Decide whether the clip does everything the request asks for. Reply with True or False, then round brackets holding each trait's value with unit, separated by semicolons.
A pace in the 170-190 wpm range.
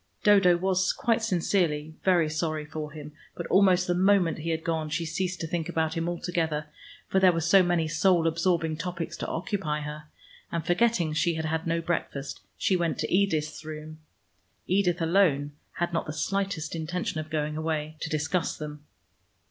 True (180 wpm)